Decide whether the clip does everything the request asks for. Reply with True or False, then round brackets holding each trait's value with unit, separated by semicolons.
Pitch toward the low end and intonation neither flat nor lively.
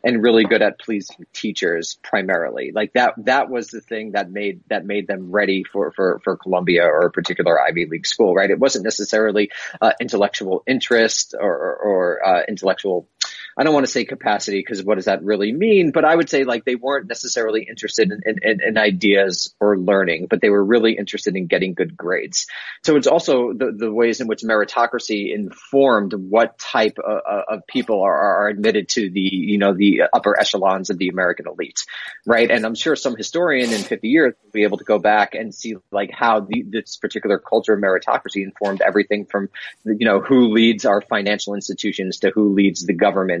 False (105 Hz; 2.3 semitones)